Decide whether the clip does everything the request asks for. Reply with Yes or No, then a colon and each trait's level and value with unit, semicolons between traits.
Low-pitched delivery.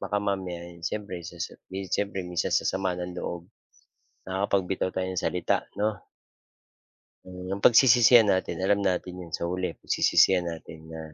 Yes: very low, 95 Hz